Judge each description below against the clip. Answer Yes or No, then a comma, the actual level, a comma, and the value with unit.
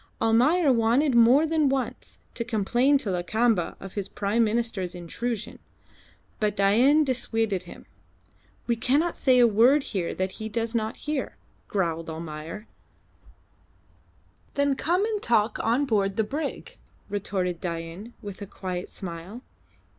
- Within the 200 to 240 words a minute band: No, slow, 135 wpm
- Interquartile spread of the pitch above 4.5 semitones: Yes, average, 5.0 semitones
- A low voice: No, high, 225 Hz